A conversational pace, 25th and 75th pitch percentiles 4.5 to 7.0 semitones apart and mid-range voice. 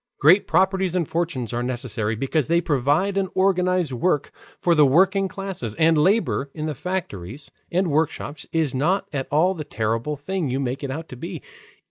Yes: average, 180 wpm; wide, 5.5 semitones; medium, 155 Hz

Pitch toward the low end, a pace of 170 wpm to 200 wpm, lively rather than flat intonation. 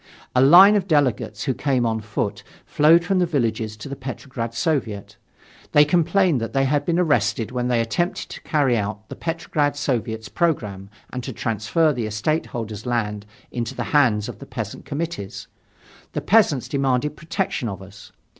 Yes: low, 130 Hz; average, 175 wpm; wide, 5.8 semitones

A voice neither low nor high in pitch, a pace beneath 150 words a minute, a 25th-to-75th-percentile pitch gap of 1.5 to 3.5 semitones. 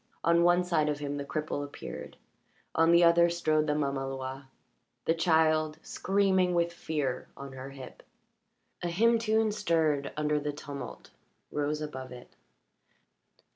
Yes: medium, 155 Hz; average, 140 wpm; average, 3.2 semitones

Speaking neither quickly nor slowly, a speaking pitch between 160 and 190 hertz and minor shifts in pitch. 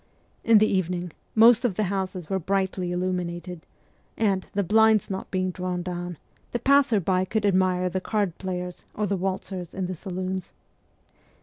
Yes: average, 165 wpm; medium, 185 Hz; narrow, 2.0 semitones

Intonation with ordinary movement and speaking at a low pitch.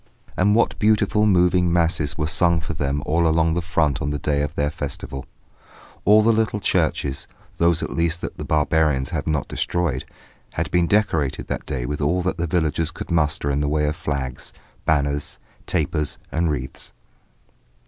Yes: average, 3.2 semitones; very low, 80 Hz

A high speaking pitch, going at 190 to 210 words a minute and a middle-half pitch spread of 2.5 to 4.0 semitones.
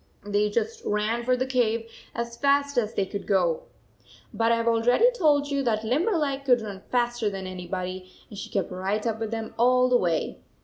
Yes: high, 230 Hz; average, 195 wpm; average, 3.7 semitones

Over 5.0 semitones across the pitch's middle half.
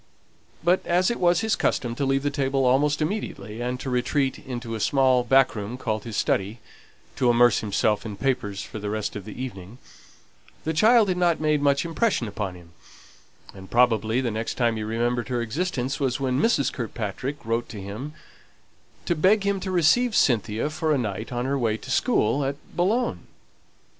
Yes: wide, 5.4 semitones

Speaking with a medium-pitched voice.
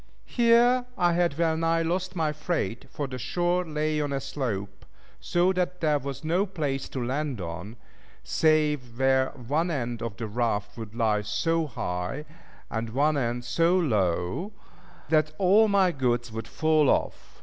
Yes: medium, 145 Hz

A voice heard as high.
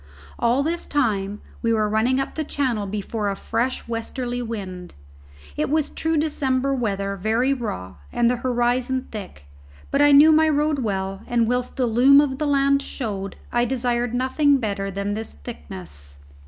Yes: high, 240 Hz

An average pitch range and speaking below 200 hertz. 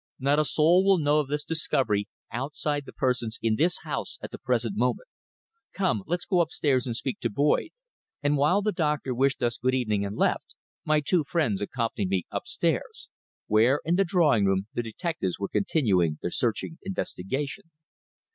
No: wide, 6.0 semitones; low, 135 Hz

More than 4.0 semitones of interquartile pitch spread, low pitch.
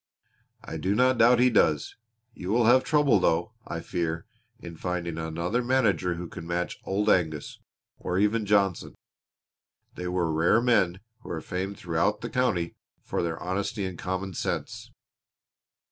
Yes: average, 4.6 semitones; very low, 95 Hz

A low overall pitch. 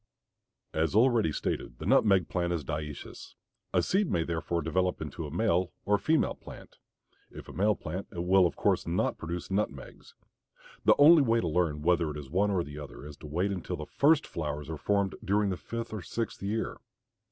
Yes: very low, 90 Hz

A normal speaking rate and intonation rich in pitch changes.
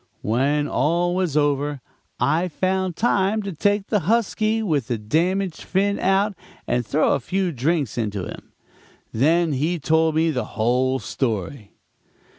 Yes: average, 145 wpm; wide, 6.3 semitones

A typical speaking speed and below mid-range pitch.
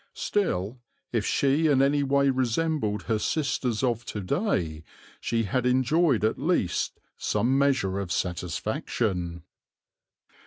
No: slow, 120 wpm; low, 125 Hz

